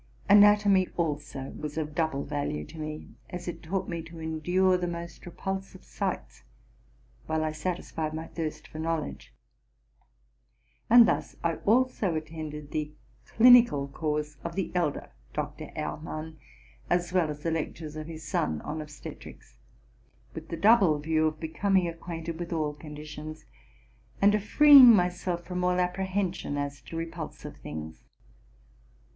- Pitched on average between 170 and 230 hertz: No, medium, 160 Hz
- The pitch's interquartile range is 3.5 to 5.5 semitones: No, average, 3.0 semitones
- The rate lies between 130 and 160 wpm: Yes, average, 145 wpm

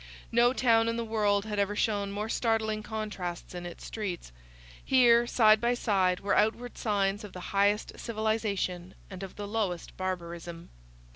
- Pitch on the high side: Yes, high, 210 Hz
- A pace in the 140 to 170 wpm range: Yes, average, 160 wpm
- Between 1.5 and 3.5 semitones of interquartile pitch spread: Yes, average, 3.0 semitones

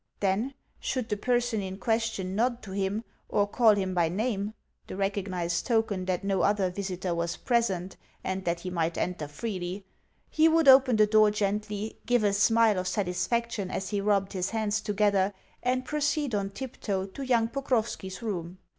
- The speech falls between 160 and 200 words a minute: Yes, average, 170 wpm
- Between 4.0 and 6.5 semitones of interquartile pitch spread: No, average, 3.4 semitones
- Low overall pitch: No, high, 205 Hz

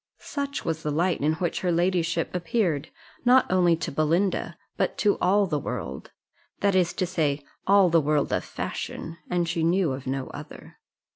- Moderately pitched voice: Yes, medium, 170 Hz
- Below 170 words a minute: No, average, 175 wpm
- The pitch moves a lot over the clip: No, average, 3.2 semitones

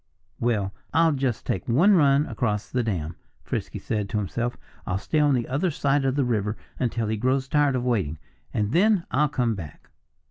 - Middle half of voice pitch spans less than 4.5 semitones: No, average, 5.3 semitones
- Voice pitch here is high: No, low, 125 Hz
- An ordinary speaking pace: Yes, average, 190 wpm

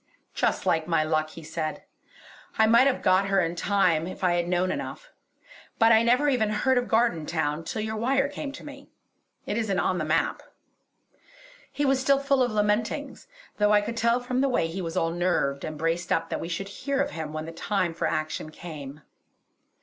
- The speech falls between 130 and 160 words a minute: No, fast, 205 wpm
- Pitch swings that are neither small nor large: No, wide, 6.6 semitones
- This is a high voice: Yes, high, 195 Hz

